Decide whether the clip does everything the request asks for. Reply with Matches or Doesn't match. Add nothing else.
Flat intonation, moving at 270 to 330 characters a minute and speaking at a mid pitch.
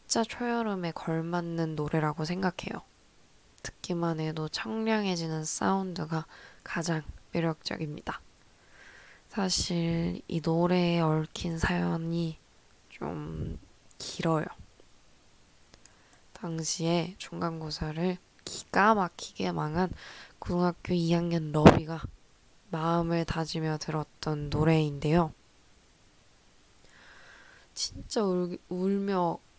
Doesn't match